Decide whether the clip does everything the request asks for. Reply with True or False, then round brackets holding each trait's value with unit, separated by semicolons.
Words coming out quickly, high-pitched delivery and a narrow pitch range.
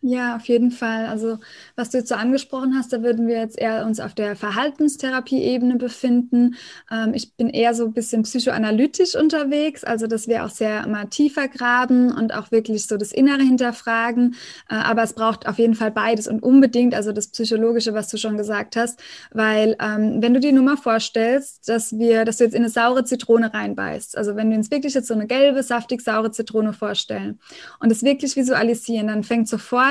True (205 wpm; 230 Hz; 2.3 semitones)